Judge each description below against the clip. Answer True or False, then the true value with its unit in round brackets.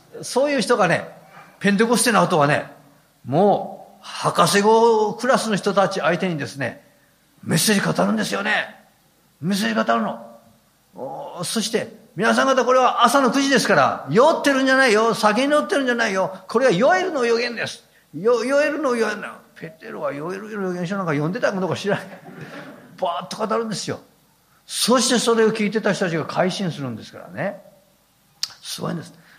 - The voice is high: True (200 Hz)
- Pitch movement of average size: True (4.9 semitones)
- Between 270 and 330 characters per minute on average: False (355 characters per minute)